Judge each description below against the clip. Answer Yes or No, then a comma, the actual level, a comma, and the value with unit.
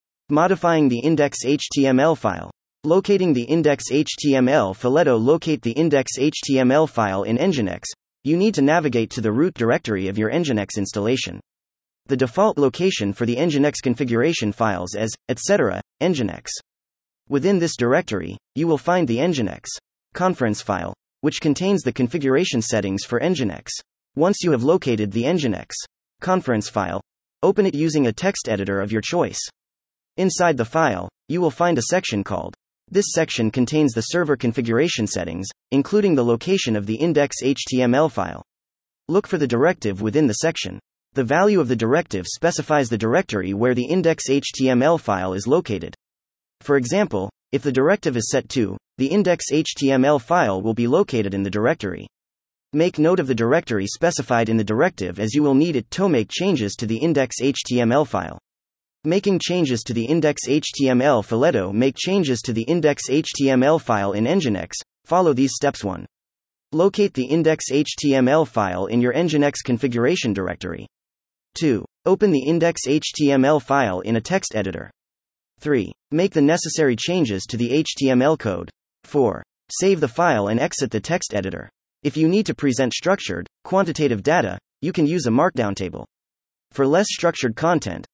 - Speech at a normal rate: Yes, average, 155 wpm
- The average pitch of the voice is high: No, low, 130 Hz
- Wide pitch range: Yes, wide, 7.2 semitones